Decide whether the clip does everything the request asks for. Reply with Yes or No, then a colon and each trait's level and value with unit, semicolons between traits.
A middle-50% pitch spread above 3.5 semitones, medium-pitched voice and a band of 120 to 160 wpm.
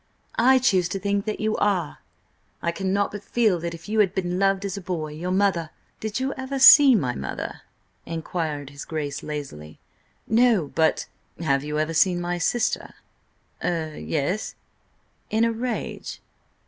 Yes: average, 5.1 semitones; medium, 180 Hz; average, 155 wpm